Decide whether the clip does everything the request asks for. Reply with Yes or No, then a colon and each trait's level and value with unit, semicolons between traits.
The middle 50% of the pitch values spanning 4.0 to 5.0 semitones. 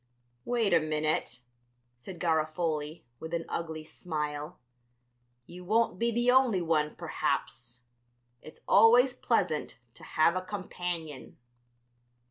Yes: average, 4.4 semitones